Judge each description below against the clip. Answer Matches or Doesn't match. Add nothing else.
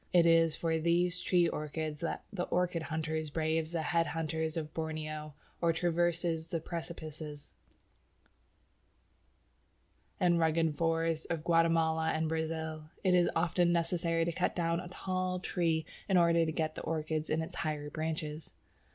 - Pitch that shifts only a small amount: Matches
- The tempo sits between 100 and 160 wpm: Matches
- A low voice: Doesn't match